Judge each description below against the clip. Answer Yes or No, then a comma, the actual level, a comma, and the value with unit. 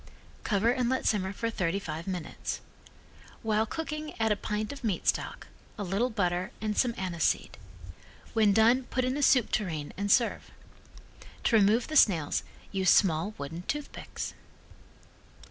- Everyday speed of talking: Yes, average, 155 wpm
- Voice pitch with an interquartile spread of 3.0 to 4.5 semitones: Yes, average, 4.1 semitones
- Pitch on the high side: Yes, high, 210 Hz